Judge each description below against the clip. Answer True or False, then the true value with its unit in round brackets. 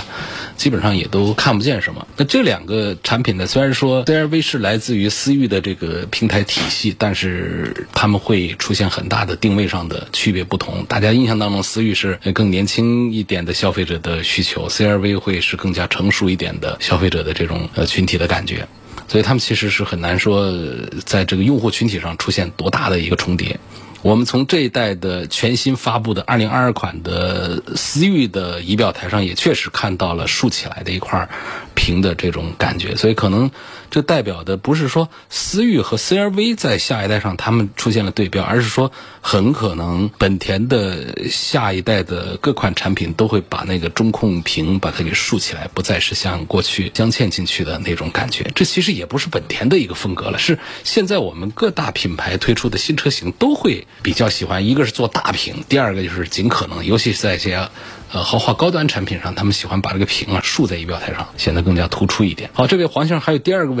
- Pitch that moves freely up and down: False (4.6 semitones)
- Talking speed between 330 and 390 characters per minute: False (320 characters per minute)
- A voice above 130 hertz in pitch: False (105 Hz)